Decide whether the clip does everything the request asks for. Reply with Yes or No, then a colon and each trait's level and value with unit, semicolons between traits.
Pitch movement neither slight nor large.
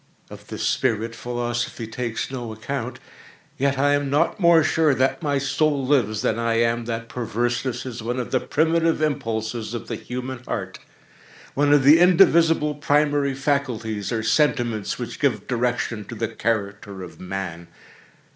Yes: average, 4.1 semitones